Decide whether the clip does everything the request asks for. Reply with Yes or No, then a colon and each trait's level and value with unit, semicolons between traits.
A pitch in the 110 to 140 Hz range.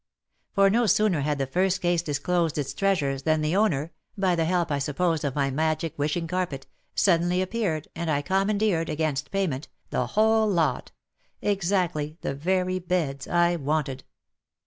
No: medium, 170 Hz